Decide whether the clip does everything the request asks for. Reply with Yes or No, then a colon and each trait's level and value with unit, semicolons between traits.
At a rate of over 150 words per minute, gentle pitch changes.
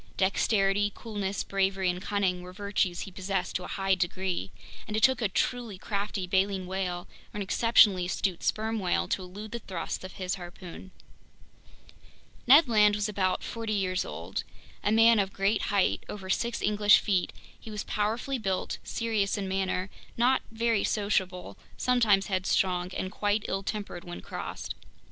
Yes: average, 160 wpm; narrow, 2.3 semitones